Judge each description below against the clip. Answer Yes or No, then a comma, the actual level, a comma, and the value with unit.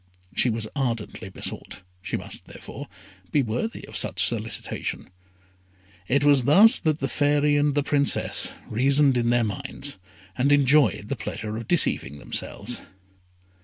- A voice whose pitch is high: No, low, 135 Hz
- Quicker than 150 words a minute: No, average, 145 wpm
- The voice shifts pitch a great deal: No, average, 3.9 semitones